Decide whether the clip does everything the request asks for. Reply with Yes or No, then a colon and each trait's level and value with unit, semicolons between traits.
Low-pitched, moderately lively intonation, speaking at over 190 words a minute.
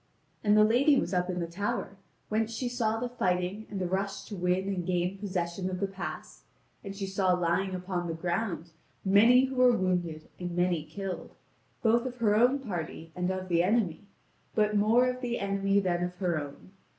No: high, 195 Hz; average, 3.4 semitones; average, 200 wpm